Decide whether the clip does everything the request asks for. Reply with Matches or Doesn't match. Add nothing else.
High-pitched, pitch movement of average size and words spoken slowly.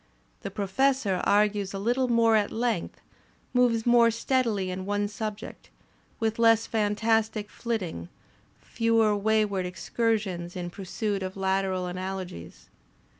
Matches